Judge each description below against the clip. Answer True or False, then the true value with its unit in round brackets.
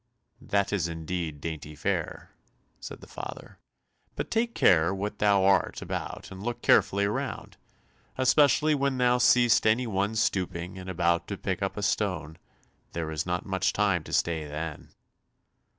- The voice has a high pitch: False (95 Hz)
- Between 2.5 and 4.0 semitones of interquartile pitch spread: False (4.9 semitones)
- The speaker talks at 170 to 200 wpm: False (155 wpm)